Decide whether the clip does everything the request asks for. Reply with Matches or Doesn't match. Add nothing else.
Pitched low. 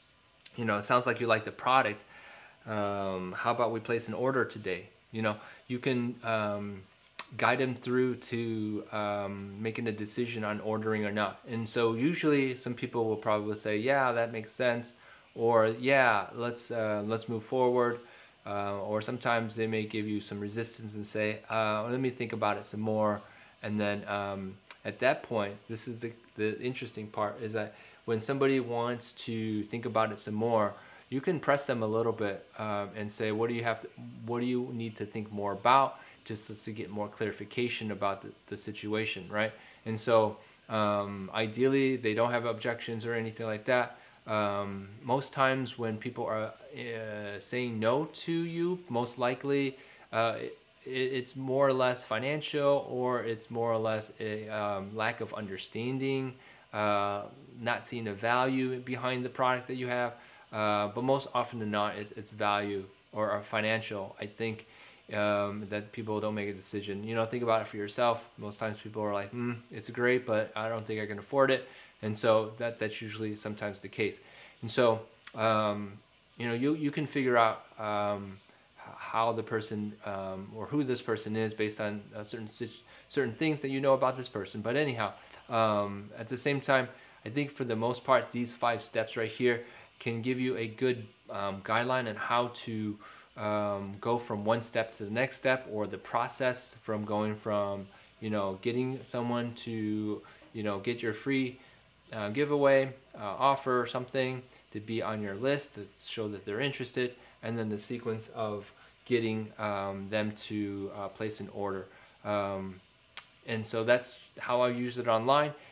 Matches